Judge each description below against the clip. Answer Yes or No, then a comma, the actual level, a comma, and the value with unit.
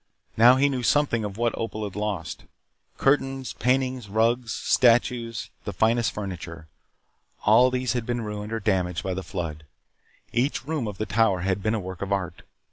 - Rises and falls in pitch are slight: No, average, 4.0 semitones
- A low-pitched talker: Yes, low, 110 Hz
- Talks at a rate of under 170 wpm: No, average, 175 wpm